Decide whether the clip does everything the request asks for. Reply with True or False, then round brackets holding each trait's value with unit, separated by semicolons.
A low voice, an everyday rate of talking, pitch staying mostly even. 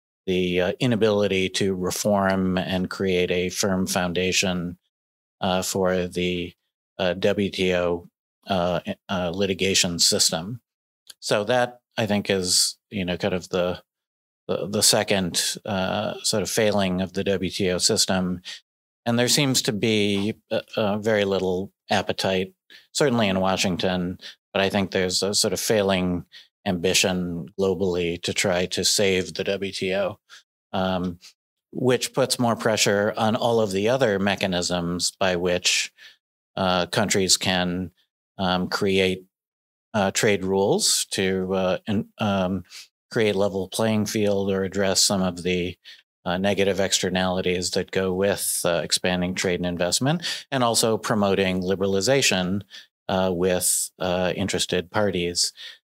False (95 Hz; 130 wpm; 1.9 semitones)